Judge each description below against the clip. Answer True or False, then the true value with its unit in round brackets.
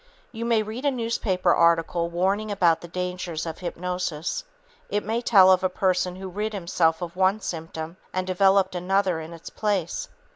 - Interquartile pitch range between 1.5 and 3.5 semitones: True (2.9 semitones)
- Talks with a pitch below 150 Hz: False (185 Hz)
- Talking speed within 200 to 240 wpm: False (175 wpm)